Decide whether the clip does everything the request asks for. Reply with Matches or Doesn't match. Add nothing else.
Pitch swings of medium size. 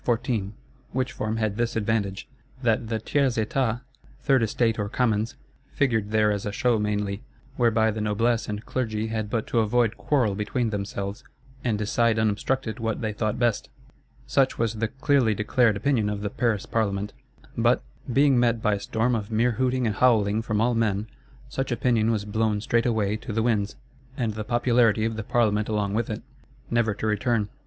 Doesn't match